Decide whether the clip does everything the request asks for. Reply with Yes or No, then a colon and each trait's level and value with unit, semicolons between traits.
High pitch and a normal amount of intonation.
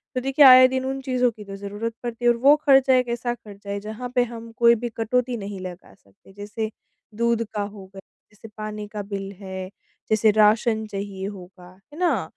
Yes: high, 220 Hz; average, 3.4 semitones